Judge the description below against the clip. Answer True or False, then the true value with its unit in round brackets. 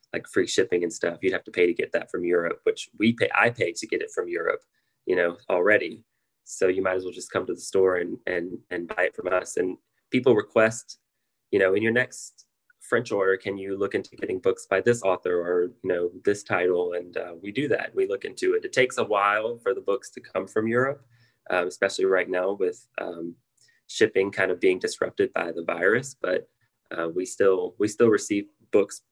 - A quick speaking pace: True (225 wpm)